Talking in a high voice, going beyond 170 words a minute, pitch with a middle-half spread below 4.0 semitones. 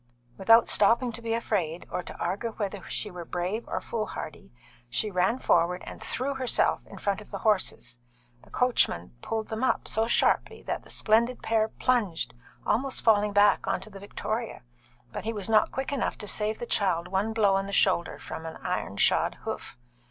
Yes: high, 210 Hz; average, 190 wpm; average, 3.2 semitones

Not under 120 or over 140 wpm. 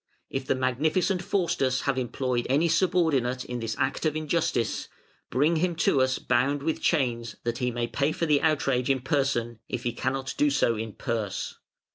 No: average, 180 wpm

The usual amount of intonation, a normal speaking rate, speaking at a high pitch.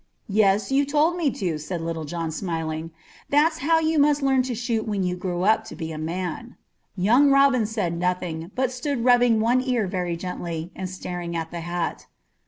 No: wide, 6.9 semitones; average, 190 wpm; high, 195 Hz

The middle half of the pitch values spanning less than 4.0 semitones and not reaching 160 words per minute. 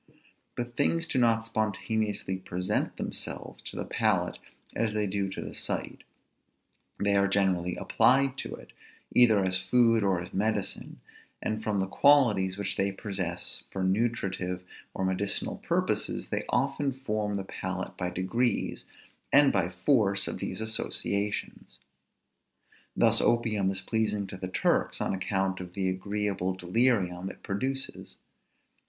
Yes: average, 3.1 semitones; average, 140 wpm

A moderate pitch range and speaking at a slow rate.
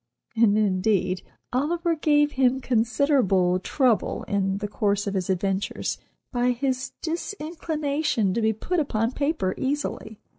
No: wide, 6.4 semitones; slow, 125 wpm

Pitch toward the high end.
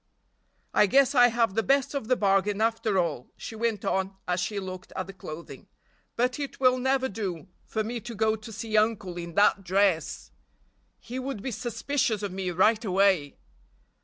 Yes: high, 215 Hz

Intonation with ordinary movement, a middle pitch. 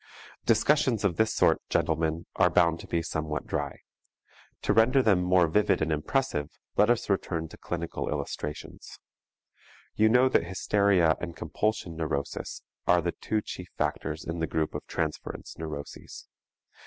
No: average, 4.7 semitones; very low, 85 Hz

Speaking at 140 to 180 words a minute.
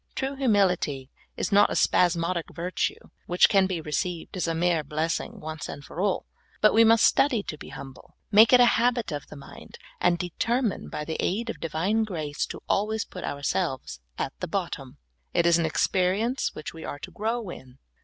No: average, 190 wpm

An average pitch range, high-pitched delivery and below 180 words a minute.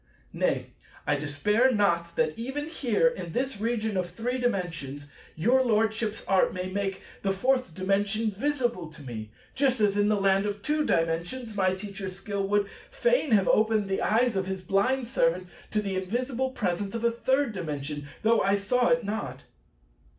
Yes: average, 4.5 semitones; high, 205 Hz; average, 170 wpm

